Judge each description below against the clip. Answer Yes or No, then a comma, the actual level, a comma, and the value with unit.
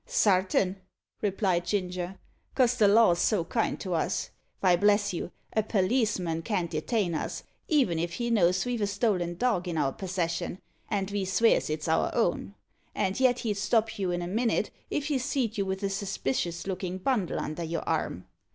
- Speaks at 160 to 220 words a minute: Yes, average, 180 wpm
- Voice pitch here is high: Yes, high, 195 Hz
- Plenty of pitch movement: No, average, 4.0 semitones